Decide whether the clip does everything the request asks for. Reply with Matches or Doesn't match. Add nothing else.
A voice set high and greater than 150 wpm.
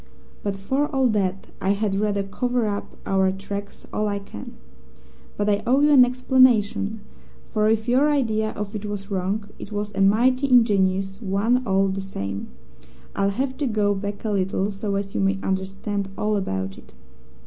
Matches